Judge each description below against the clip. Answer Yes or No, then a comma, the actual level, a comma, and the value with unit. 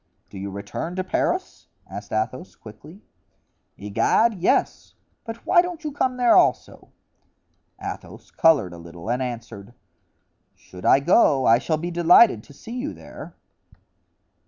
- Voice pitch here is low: No, medium, 145 Hz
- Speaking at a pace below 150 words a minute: Yes, average, 140 wpm